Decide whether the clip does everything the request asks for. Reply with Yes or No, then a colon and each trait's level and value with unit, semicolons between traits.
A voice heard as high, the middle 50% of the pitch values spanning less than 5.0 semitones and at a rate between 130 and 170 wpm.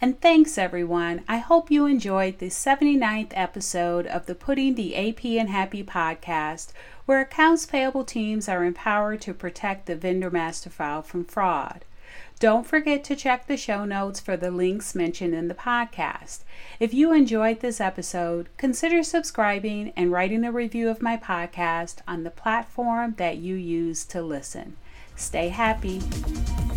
No: high, 200 Hz; wide, 5.5 semitones; average, 155 wpm